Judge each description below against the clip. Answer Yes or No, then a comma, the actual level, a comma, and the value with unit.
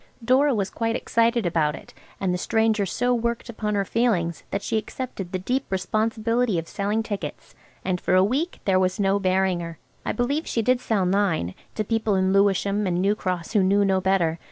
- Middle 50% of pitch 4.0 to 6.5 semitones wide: No, average, 3.5 semitones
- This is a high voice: Yes, high, 200 Hz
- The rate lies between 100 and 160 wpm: No, fast, 205 wpm